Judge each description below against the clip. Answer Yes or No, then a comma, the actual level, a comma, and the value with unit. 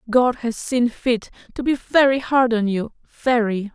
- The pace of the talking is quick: No, average, 175 wpm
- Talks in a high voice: Yes, high, 240 Hz